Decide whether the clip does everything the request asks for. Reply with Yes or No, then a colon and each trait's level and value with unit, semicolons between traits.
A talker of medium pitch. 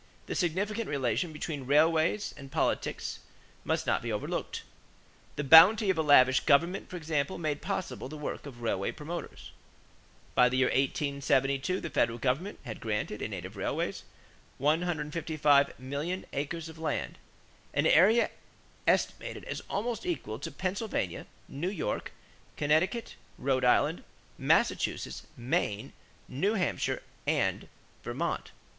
Yes: medium, 150 Hz